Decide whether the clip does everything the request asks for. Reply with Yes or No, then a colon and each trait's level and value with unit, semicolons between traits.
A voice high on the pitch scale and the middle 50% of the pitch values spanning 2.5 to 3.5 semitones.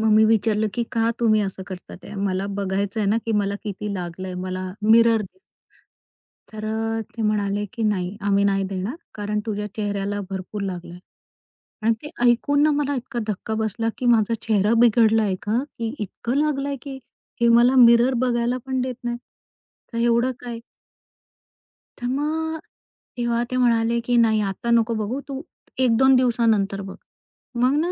Yes: high, 225 Hz; average, 3.0 semitones